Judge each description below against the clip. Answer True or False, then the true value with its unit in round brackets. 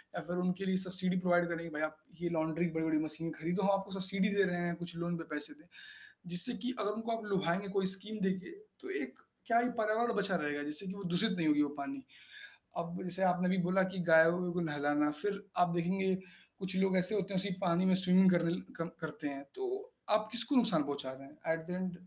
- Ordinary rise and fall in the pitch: True (3.2 semitones)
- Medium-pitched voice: True (180 Hz)